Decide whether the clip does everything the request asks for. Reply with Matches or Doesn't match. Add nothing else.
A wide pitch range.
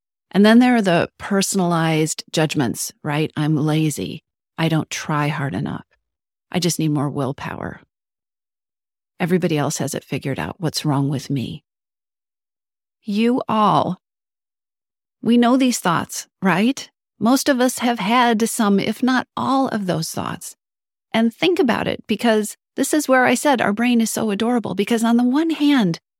Matches